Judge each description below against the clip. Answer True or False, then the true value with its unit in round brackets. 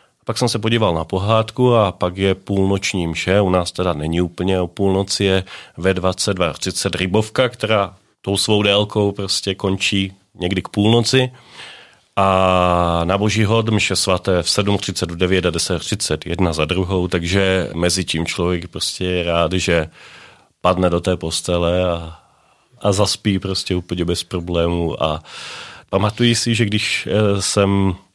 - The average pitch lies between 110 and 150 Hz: False (95 Hz)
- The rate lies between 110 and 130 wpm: False (150 wpm)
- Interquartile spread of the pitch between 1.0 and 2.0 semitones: False (2.4 semitones)